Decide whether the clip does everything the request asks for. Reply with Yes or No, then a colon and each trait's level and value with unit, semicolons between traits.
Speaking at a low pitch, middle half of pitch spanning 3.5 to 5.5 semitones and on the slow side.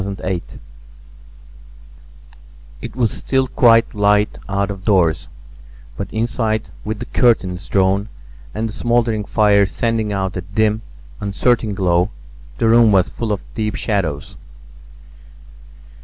No: low, 105 Hz; average, 2.7 semitones; slow, 125 wpm